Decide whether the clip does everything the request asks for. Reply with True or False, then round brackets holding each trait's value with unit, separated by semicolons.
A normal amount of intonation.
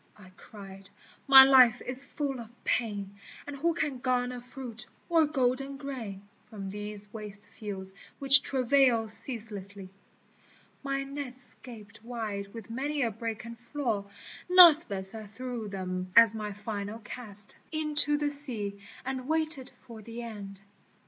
True (4.8 semitones)